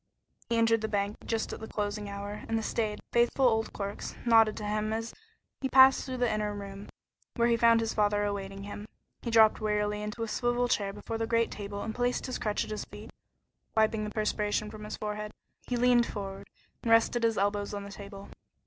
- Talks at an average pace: No, fast, 215 wpm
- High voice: Yes, high, 215 Hz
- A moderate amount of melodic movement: No, narrow, 1.8 semitones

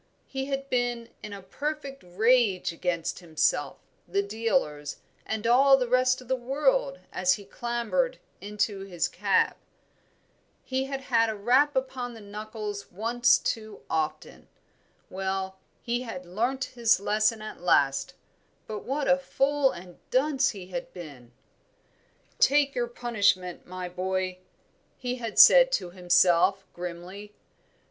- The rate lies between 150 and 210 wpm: No, slow, 135 wpm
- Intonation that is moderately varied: No, wide, 5.7 semitones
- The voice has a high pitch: Yes, high, 220 Hz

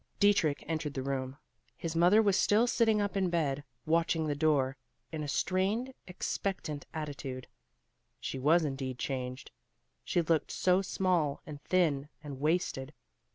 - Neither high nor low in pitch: Yes, medium, 155 Hz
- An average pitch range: Yes, average, 4.8 semitones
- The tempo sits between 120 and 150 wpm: Yes, average, 145 wpm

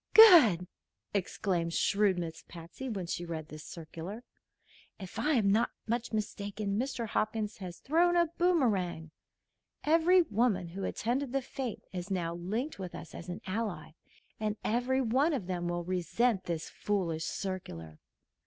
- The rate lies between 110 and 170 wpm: Yes, average, 145 wpm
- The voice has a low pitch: No, high, 200 Hz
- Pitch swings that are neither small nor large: No, wide, 5.8 semitones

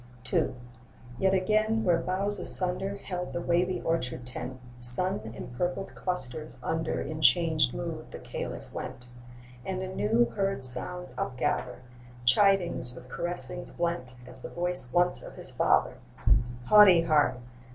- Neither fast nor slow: No, slow, 130 wpm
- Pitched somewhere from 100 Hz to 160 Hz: No, medium, 170 Hz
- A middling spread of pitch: No, wide, 6.4 semitones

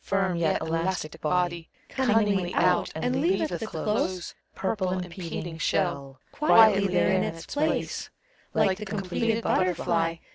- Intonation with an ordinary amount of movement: Yes, average, 3.9 semitones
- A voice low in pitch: No, medium, 185 Hz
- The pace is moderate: No, slow, 130 wpm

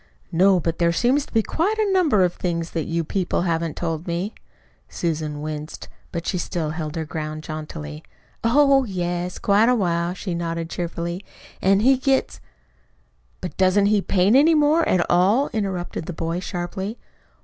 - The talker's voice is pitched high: No, medium, 175 Hz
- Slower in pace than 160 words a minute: No, average, 170 wpm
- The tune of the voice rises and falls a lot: No, average, 4.2 semitones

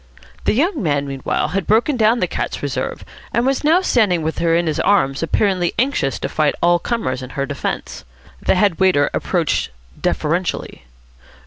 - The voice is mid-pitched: Yes, medium, 175 Hz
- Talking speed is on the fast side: No, average, 175 wpm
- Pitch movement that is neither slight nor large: No, wide, 6.9 semitones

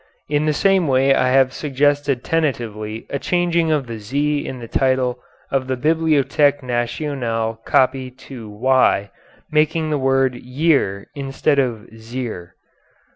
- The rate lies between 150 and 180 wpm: No, slow, 135 wpm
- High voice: No, low, 135 Hz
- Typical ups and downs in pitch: Yes, average, 3.5 semitones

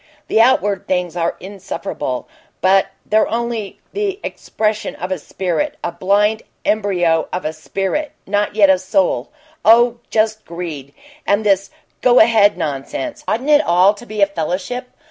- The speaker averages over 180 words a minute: No, average, 150 wpm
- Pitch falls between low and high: No, high, 200 Hz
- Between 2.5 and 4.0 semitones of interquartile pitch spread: Yes, average, 3.6 semitones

